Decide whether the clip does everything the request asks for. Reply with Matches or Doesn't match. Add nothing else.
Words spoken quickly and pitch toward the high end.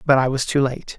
Doesn't match